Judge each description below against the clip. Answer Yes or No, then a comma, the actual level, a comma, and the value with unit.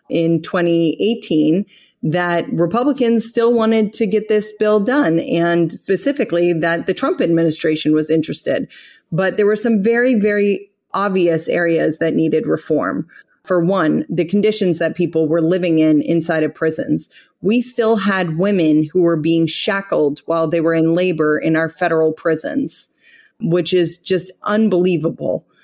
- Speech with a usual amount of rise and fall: Yes, average, 4.4 semitones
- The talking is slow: No, average, 145 wpm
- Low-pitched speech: No, medium, 175 Hz